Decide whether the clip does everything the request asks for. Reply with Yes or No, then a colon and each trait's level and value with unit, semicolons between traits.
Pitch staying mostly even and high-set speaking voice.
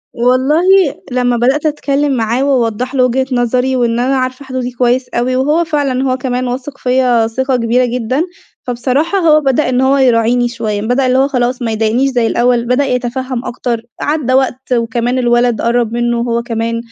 Yes: narrow, 1.7 semitones; very high, 250 Hz